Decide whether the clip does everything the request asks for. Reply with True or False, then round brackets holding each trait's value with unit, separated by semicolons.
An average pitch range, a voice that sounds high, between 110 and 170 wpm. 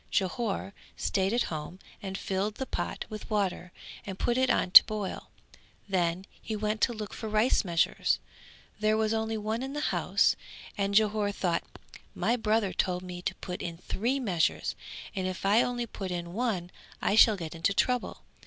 False (3.2 semitones; 205 Hz; 180 wpm)